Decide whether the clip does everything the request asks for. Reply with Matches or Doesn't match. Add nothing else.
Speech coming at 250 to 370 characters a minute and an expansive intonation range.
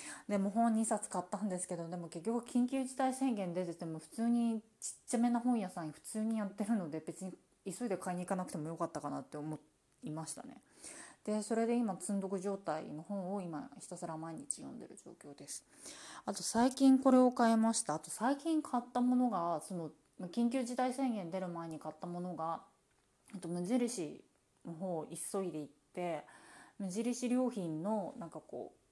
Matches